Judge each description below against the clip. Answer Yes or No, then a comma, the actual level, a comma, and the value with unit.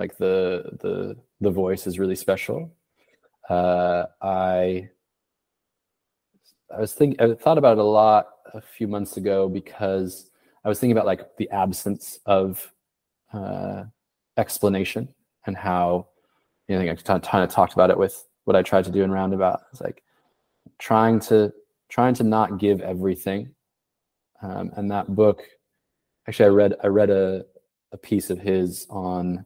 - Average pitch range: No, narrow, 2.3 semitones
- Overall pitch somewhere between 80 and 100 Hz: Yes, very low, 95 Hz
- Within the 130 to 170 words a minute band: Yes, average, 155 wpm